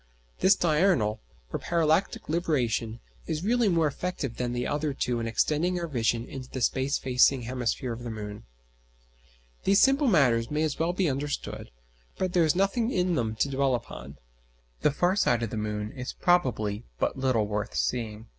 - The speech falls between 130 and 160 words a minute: No, average, 175 wpm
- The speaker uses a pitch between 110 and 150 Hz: Yes, low, 135 Hz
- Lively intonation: Yes, wide, 6.9 semitones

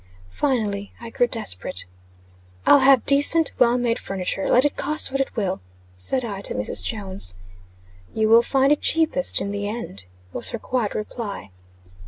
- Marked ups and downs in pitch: No, average, 5.0 semitones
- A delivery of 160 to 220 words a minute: Yes, average, 165 wpm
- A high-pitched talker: Yes, high, 230 Hz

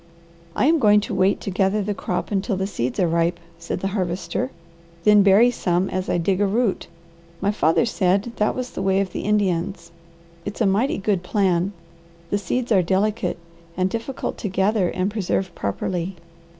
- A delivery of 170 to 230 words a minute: Yes, average, 185 wpm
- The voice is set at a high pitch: Yes, high, 195 Hz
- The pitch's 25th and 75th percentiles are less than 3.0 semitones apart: Yes, narrow, 2.5 semitones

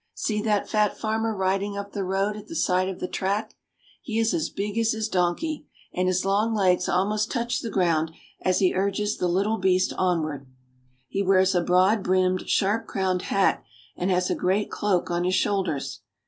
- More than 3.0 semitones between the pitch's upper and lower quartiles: No, narrow, 2.5 semitones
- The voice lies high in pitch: Yes, high, 195 Hz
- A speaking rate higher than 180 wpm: Yes, average, 190 wpm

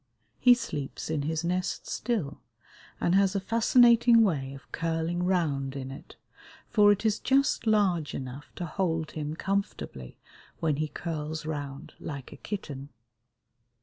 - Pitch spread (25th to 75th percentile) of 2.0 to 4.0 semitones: No, wide, 5.5 semitones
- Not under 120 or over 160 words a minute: Yes, average, 145 wpm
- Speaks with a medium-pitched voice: Yes, medium, 165 Hz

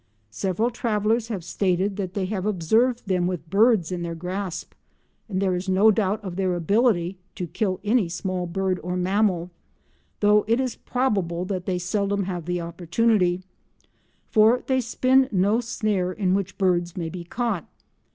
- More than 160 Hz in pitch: Yes, high, 190 Hz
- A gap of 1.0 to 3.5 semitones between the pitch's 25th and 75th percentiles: Yes, average, 3.2 semitones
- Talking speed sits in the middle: Yes, average, 165 wpm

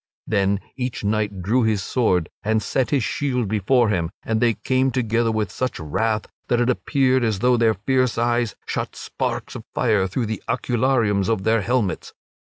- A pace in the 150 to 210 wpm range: Yes, average, 175 wpm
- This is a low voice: Yes, low, 115 Hz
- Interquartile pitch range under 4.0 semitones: Yes, average, 3.3 semitones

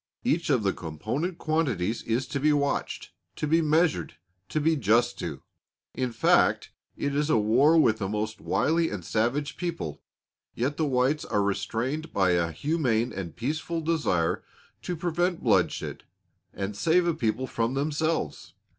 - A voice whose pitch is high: No, low, 135 Hz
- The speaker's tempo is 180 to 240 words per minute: No, average, 155 wpm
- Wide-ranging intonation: Yes, wide, 6.5 semitones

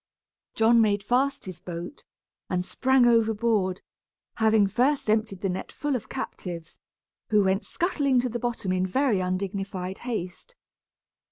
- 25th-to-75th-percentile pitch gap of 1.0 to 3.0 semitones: No, average, 4.6 semitones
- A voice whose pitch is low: No, high, 215 Hz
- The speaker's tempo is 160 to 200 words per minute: No, average, 140 wpm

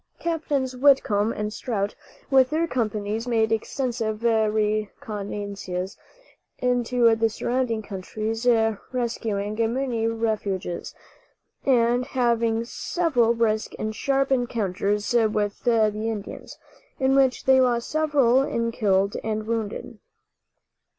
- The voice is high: Yes, high, 225 Hz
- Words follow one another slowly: Yes, slow, 105 wpm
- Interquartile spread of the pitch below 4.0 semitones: Yes, average, 2.9 semitones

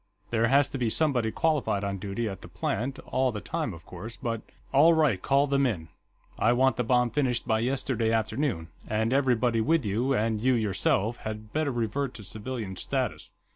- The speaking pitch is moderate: No, low, 120 Hz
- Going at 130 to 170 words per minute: No, average, 190 wpm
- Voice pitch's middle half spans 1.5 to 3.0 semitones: No, average, 3.8 semitones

